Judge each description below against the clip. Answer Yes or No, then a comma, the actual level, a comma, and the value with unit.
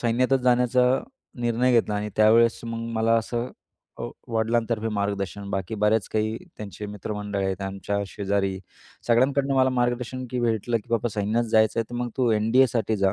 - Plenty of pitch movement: No, average, 2.8 semitones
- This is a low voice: Yes, low, 115 Hz